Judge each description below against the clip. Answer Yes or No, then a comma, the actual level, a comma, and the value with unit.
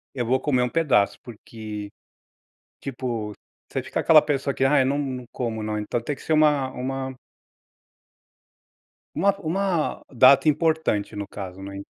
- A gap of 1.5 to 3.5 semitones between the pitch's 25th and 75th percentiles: No, average, 5.1 semitones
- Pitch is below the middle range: Yes, low, 130 Hz